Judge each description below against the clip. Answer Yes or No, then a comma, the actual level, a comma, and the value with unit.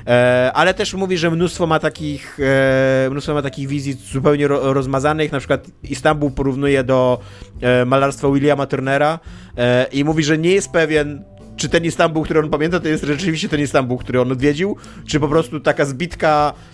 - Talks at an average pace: No, fast, 165 wpm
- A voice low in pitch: No, medium, 145 Hz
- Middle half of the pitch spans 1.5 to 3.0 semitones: Yes, average, 2.7 semitones